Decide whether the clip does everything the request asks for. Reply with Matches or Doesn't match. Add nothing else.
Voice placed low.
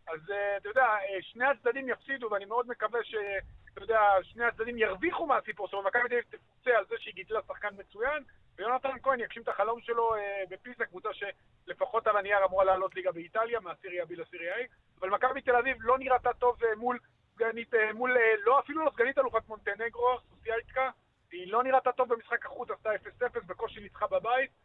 Doesn't match